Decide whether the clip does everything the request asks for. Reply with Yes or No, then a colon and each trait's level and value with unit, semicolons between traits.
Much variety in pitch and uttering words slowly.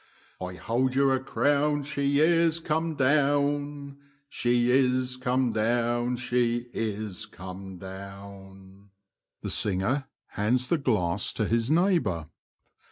Yes: wide, 5.7 semitones; slow, 100 wpm